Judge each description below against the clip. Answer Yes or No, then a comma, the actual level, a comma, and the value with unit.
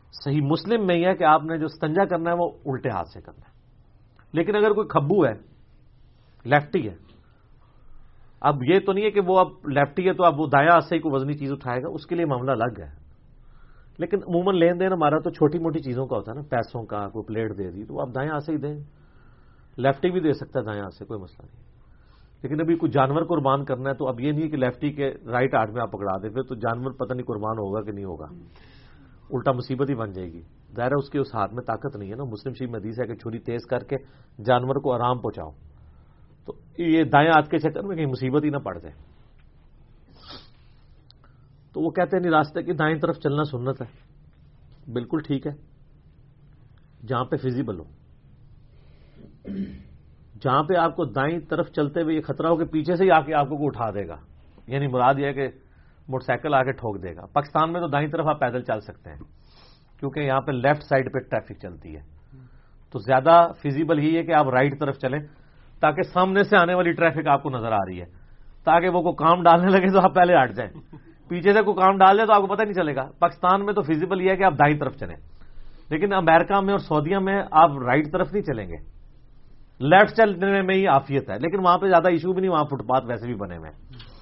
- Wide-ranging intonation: Yes, wide, 5.7 semitones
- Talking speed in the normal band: No, fast, 230 wpm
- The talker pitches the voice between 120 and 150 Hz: Yes, medium, 140 Hz